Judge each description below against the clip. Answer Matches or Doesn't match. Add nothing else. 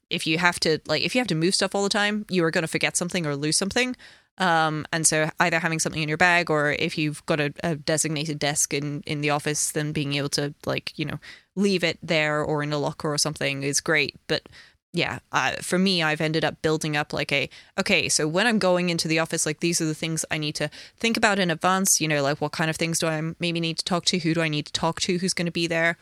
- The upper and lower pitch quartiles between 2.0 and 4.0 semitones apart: Matches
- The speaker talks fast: Matches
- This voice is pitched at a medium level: Matches